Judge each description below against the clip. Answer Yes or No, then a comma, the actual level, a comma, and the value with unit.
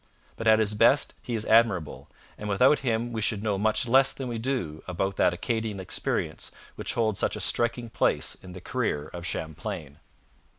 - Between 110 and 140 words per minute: No, average, 185 wpm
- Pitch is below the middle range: Yes, low, 110 Hz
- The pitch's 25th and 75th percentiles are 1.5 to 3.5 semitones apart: No, average, 4.0 semitones